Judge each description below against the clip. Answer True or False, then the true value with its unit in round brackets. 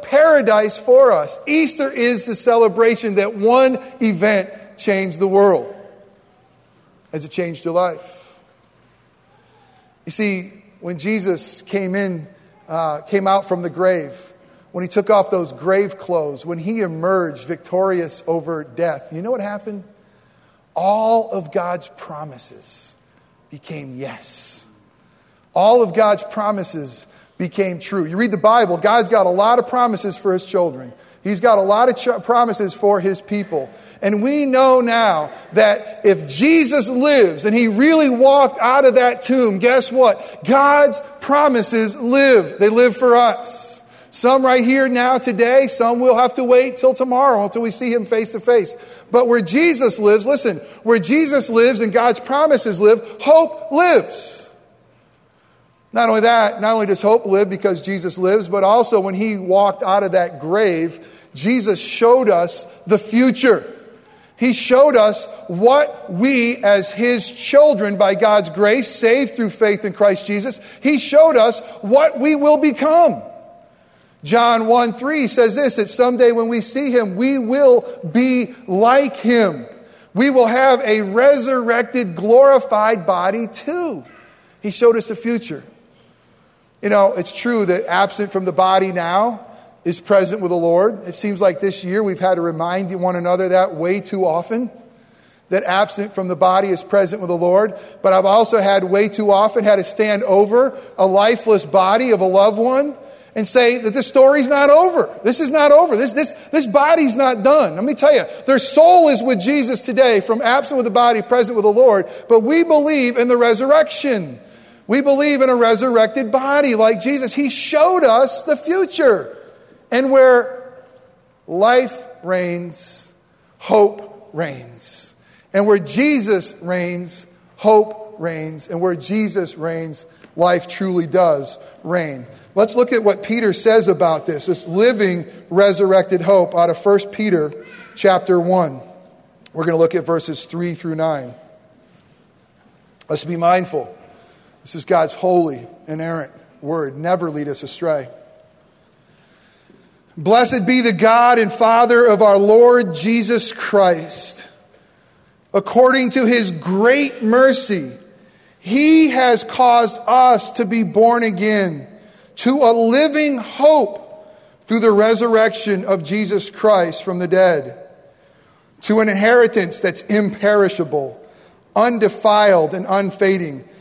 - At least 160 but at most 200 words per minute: False (150 wpm)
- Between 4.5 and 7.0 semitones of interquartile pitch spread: True (4.9 semitones)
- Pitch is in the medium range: False (215 Hz)